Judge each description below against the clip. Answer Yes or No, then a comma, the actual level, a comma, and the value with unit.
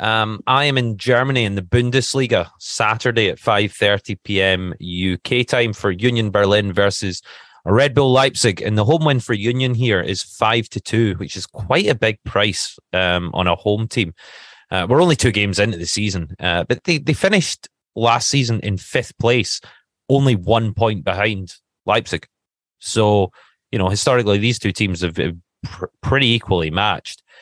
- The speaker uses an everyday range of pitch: Yes, average, 3.8 semitones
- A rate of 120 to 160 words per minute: No, average, 170 wpm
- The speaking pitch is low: Yes, low, 110 Hz